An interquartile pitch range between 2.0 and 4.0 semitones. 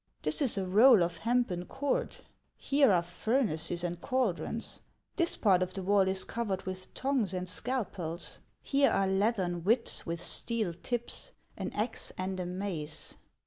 No: average, 5.0 semitones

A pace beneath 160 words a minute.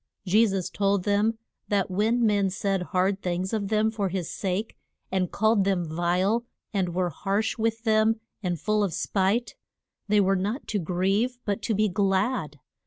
No: average, 175 wpm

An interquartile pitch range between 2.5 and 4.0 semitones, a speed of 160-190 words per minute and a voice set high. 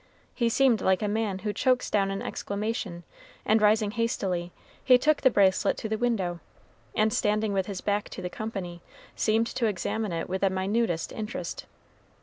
Yes: average, 3.0 semitones; average, 175 wpm; high, 210 Hz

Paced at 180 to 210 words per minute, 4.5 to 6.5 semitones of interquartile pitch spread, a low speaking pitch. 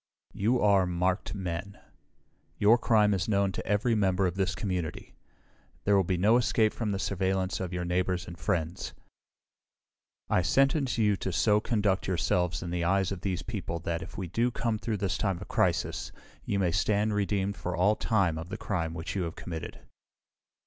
No: average, 185 wpm; average, 2.8 semitones; very low, 95 Hz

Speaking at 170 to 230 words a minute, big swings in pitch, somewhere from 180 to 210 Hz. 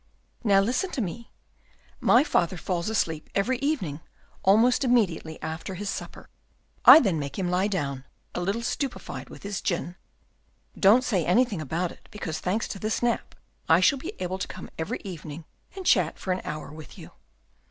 Yes: average, 175 wpm; wide, 5.9 semitones; high, 190 Hz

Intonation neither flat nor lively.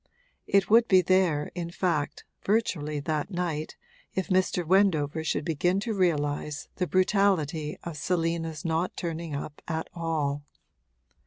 Yes: average, 3.4 semitones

